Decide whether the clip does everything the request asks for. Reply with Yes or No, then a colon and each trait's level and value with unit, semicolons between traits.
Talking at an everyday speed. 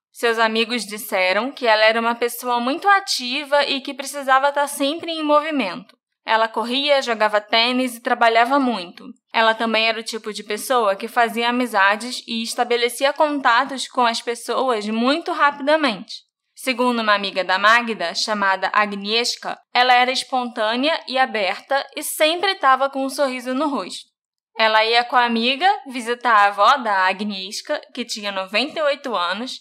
Yes: average, 155 wpm